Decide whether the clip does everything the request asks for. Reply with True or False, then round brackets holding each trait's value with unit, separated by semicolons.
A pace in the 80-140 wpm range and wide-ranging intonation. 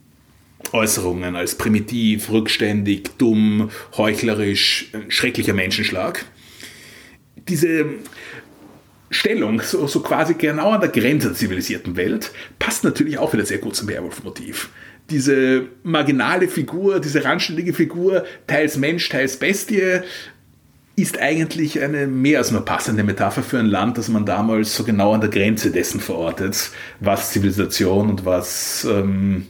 True (130 wpm; 7.0 semitones)